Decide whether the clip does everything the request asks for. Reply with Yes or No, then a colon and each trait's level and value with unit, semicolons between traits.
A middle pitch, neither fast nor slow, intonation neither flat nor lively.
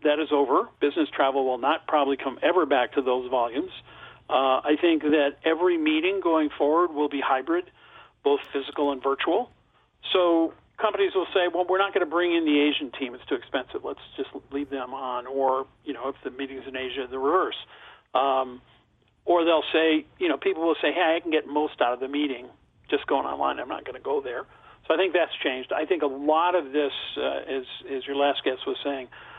No: medium, 145 Hz; fast, 220 wpm; average, 4.0 semitones